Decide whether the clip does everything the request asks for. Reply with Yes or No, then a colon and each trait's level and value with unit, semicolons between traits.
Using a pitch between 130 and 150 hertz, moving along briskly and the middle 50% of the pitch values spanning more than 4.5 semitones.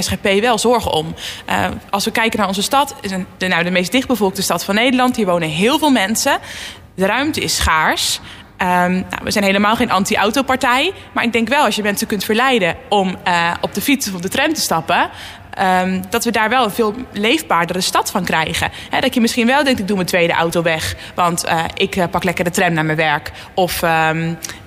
No: high, 200 Hz; fast, 220 wpm; average, 4.9 semitones